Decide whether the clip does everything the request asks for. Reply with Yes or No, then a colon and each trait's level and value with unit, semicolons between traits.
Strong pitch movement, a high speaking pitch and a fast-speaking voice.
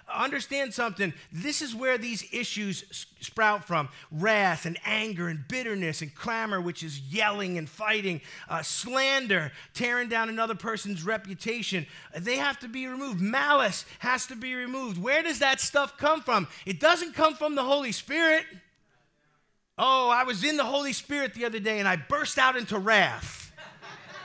No: wide, 5.7 semitones; high, 225 Hz; average, 165 wpm